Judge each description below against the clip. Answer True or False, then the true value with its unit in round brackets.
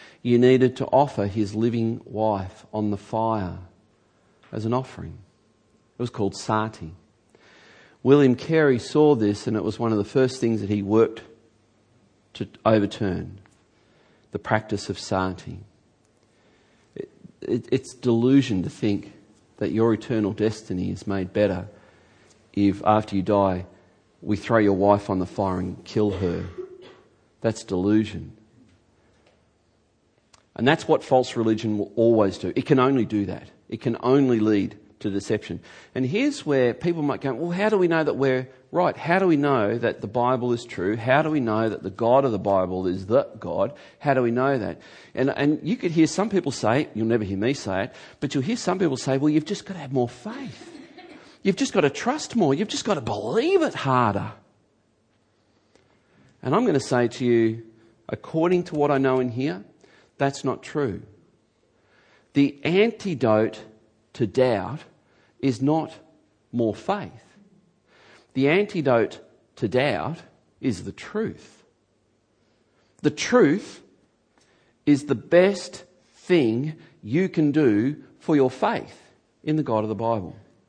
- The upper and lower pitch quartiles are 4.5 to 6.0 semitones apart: True (5.1 semitones)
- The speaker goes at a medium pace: True (160 wpm)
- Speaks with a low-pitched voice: True (115 Hz)